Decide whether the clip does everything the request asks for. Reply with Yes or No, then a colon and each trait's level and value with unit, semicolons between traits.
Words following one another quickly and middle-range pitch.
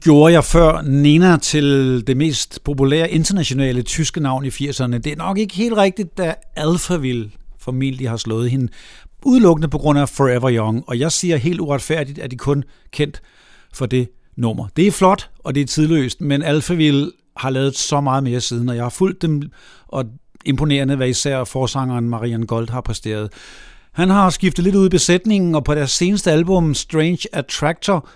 No: average, 185 wpm; medium, 145 Hz